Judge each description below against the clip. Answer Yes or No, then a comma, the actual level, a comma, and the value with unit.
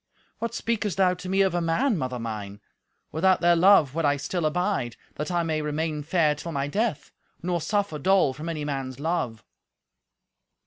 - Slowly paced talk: No, average, 180 wpm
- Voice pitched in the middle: Yes, medium, 165 Hz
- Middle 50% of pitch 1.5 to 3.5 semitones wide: No, average, 4.3 semitones